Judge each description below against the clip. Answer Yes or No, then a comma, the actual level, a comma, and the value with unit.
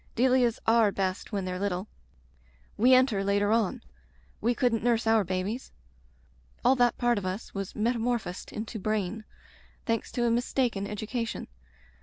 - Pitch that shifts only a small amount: No, average, 3.2 semitones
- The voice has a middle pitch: No, high, 220 Hz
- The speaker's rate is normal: Yes, average, 150 wpm